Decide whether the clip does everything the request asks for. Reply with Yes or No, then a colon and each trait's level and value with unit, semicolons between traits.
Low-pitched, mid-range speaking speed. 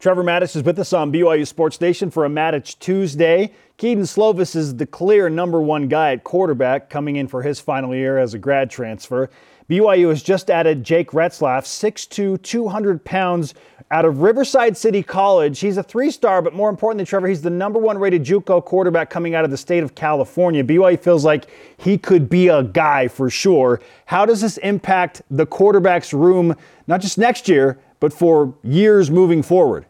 No: medium, 175 Hz; average, 190 wpm